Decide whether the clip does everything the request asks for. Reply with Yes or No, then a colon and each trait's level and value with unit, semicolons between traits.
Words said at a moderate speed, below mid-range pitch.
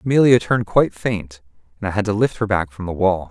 No: fast, 255 wpm; low, 100 Hz